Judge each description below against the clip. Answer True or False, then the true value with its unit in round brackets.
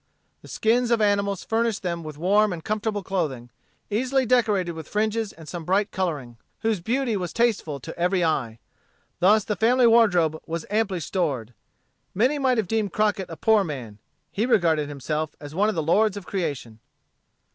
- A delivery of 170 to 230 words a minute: True (175 wpm)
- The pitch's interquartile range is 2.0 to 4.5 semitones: False (5.4 semitones)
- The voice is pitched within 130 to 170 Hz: False (195 Hz)